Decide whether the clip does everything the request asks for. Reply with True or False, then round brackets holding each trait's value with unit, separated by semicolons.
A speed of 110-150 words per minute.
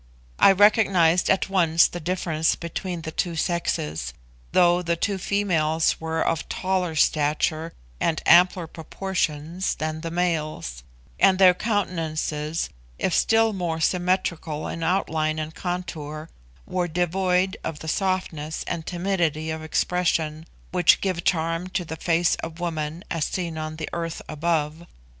True (140 wpm)